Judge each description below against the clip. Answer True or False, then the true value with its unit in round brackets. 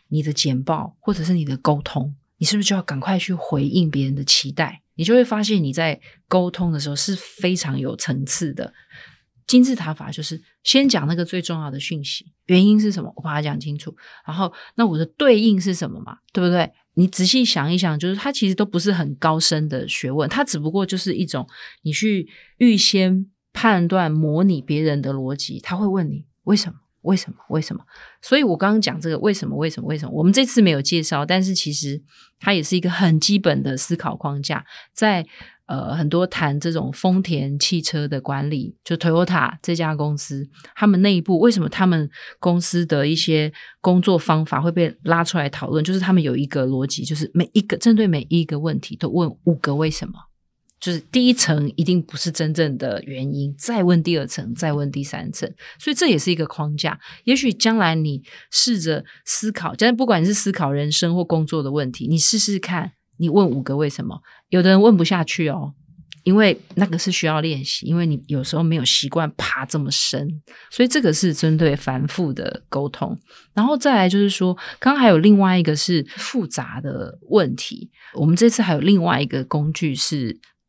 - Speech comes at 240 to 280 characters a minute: False (300 characters per minute)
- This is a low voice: False (165 Hz)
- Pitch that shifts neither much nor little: True (4.1 semitones)